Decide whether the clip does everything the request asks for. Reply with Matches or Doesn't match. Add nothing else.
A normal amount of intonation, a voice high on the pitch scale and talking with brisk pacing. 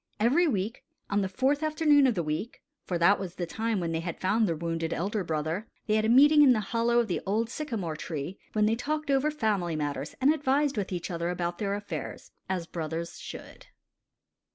Doesn't match